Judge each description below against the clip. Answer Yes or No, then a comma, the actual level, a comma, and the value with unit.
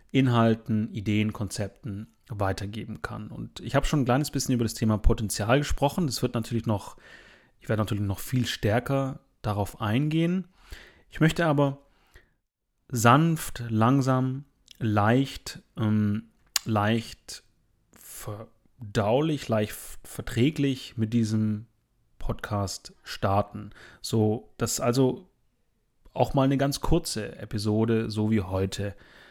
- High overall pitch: No, low, 115 Hz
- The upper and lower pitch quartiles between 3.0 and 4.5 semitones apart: Yes, average, 4.0 semitones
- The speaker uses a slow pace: Yes, slow, 115 wpm